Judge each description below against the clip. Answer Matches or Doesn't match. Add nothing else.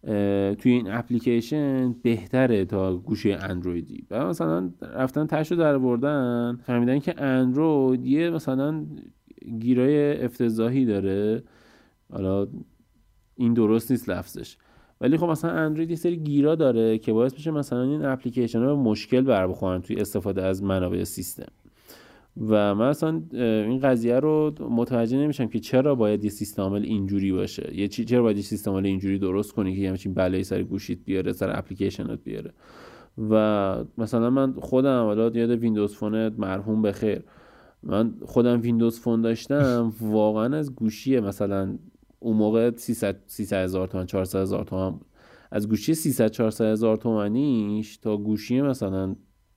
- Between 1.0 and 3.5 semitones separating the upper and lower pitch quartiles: Doesn't match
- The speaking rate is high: Doesn't match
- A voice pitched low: Matches